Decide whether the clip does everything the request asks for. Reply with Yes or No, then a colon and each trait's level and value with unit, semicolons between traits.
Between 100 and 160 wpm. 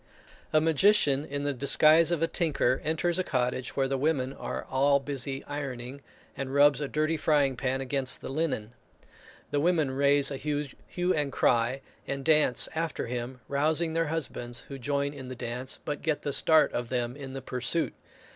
No: average, 180 wpm